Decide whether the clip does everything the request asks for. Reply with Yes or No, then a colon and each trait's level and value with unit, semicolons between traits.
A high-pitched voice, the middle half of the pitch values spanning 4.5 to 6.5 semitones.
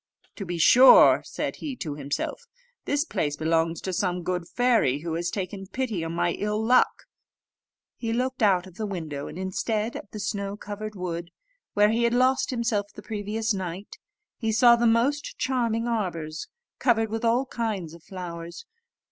Yes: high, 205 Hz; average, 5.1 semitones